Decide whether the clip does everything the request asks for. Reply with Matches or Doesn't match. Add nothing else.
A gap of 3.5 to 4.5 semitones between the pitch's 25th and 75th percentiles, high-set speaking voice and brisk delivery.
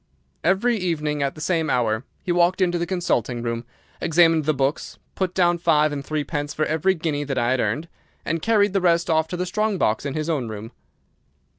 Doesn't match